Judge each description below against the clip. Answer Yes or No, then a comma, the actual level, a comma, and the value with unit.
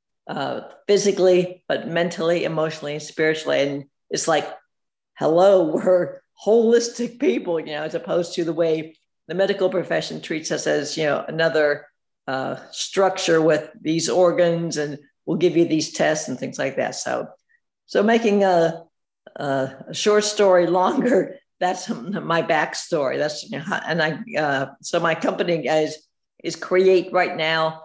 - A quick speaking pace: No, average, 155 wpm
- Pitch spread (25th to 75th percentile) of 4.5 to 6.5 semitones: No, average, 3.1 semitones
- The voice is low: No, medium, 170 Hz